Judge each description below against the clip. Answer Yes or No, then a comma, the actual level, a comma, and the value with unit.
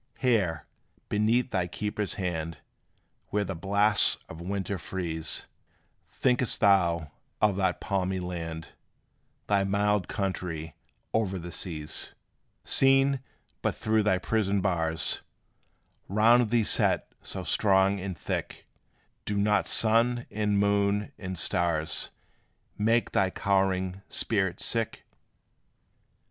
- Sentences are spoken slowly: Yes, slow, 110 wpm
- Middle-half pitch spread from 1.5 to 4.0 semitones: Yes, average, 2.9 semitones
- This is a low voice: Yes, low, 100 Hz